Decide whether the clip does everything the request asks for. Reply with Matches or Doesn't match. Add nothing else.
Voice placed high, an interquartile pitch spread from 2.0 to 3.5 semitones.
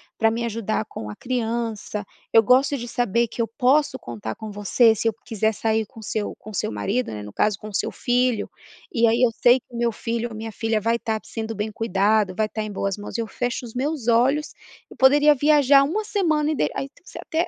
Matches